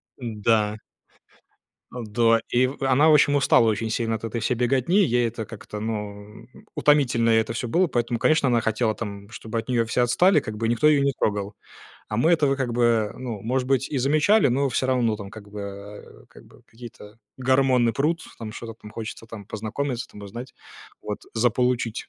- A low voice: Yes, low, 115 Hz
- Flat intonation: No, average, 3.1 semitones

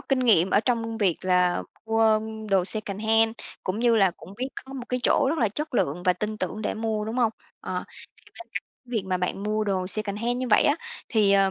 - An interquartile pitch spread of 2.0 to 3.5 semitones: Yes, average, 3.2 semitones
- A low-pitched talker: No, high, 215 Hz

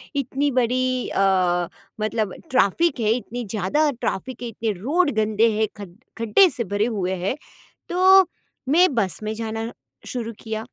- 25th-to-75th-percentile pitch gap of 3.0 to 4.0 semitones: Yes, average, 3.7 semitones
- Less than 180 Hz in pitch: No, high, 230 Hz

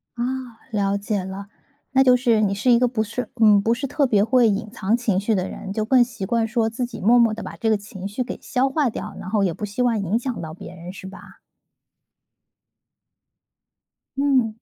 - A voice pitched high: Yes, high, 220 Hz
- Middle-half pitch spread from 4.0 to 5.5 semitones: No, average, 3.4 semitones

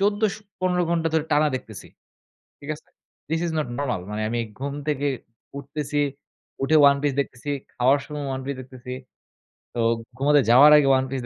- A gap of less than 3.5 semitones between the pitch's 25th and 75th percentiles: Yes, average, 2.8 semitones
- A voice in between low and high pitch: Yes, medium, 145 Hz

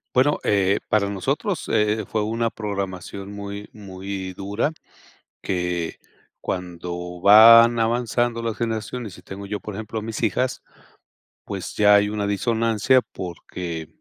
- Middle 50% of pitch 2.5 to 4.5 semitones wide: Yes, average, 2.9 semitones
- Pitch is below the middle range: Yes, low, 105 Hz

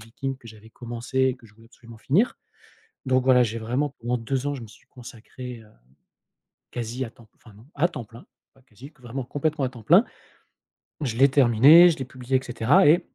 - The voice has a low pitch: Yes, low, 125 Hz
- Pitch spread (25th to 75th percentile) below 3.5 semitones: Yes, average, 2.9 semitones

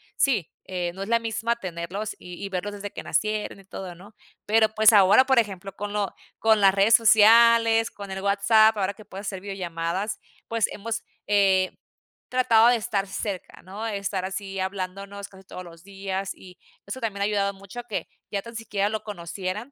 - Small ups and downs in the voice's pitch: Yes, narrow, 2.3 semitones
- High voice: Yes, high, 200 Hz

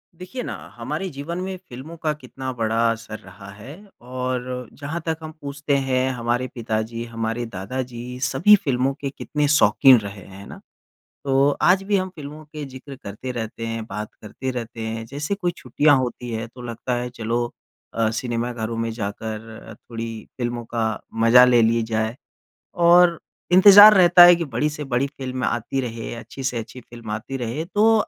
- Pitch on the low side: Yes, low, 125 Hz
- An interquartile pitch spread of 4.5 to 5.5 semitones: No, average, 4.1 semitones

